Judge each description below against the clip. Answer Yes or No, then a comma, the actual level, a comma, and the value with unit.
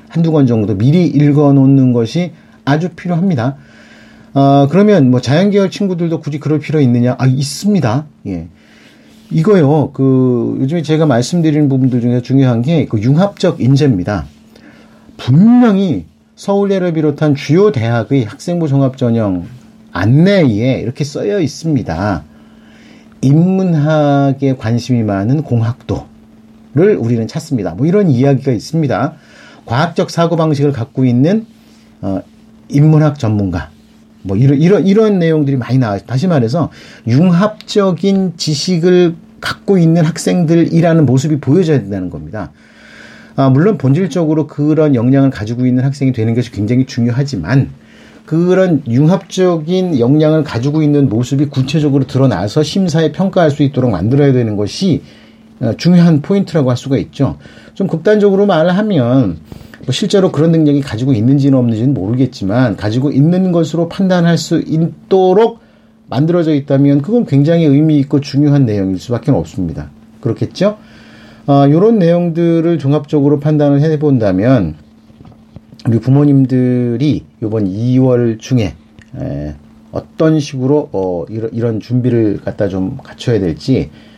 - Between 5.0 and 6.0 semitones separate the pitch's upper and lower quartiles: Yes, wide, 5.4 semitones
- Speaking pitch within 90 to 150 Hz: Yes, medium, 140 Hz